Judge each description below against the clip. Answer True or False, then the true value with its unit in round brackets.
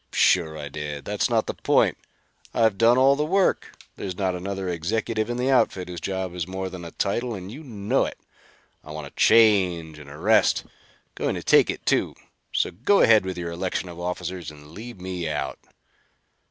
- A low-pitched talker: True (95 Hz)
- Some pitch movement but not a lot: True (4.8 semitones)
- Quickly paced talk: False (195 wpm)